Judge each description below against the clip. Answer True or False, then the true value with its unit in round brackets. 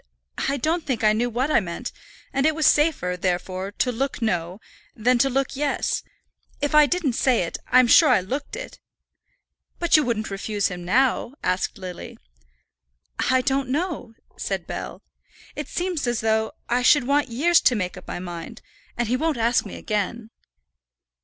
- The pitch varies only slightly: False (5.2 semitones)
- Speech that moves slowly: False (175 wpm)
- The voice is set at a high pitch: True (245 Hz)